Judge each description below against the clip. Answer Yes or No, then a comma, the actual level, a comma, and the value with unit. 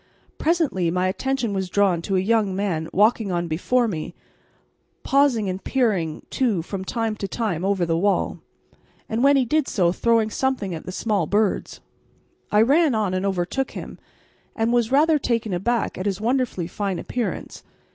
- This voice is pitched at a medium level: No, high, 210 Hz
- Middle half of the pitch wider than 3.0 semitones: Yes, average, 4.6 semitones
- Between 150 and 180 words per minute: Yes, average, 170 wpm